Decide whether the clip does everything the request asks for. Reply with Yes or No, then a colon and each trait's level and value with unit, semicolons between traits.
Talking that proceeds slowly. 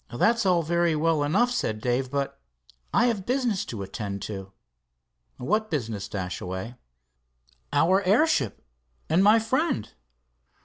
Yes: slow, 125 wpm